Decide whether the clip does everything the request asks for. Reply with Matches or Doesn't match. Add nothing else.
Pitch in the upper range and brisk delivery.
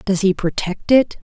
Doesn't match